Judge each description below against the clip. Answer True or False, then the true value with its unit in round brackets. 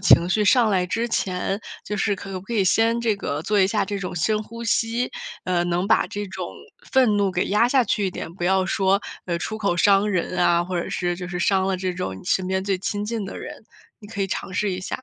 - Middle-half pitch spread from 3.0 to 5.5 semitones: False (2.6 semitones)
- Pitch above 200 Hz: False (195 Hz)